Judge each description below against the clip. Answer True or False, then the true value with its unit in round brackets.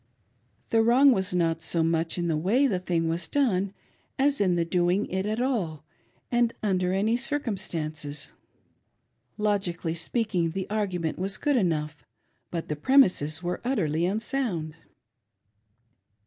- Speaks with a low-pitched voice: False (185 Hz)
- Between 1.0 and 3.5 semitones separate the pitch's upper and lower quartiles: False (5.3 semitones)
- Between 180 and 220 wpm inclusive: False (135 wpm)